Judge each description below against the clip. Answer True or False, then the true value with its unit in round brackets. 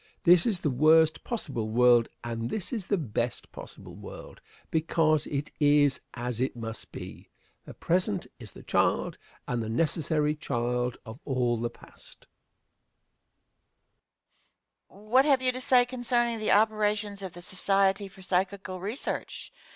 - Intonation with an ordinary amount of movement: False (8.8 semitones)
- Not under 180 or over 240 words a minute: False (145 wpm)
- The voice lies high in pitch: False (165 Hz)